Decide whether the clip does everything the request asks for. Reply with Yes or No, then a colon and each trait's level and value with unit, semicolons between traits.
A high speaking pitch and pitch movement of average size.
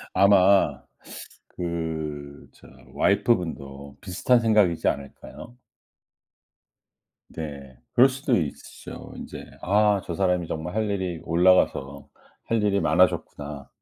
No: very low, 90 Hz; average, 5.0 semitones